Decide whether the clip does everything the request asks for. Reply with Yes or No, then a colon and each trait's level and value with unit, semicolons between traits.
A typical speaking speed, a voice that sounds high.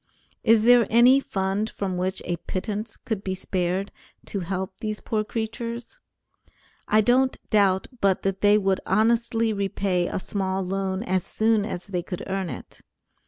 Yes: average, 160 wpm; high, 200 Hz